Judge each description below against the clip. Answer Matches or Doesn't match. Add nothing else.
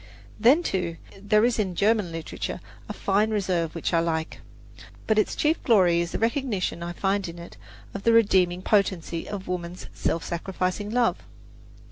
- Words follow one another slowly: Doesn't match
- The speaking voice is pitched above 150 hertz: Matches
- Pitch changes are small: Doesn't match